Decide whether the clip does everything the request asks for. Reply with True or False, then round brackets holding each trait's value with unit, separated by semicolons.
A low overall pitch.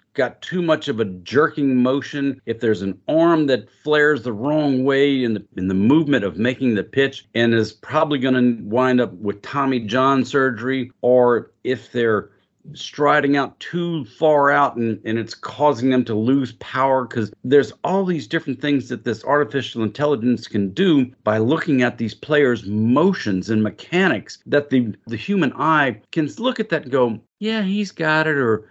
True (130 Hz)